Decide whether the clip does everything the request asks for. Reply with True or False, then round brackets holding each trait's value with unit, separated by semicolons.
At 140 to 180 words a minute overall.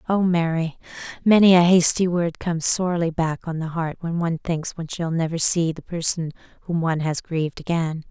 False (195 wpm)